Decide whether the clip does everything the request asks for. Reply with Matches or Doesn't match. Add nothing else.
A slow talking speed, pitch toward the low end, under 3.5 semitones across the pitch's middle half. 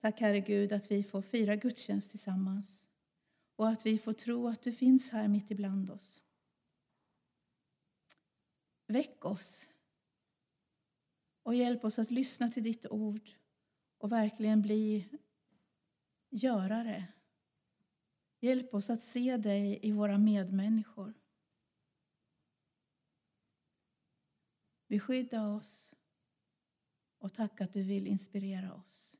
Doesn't match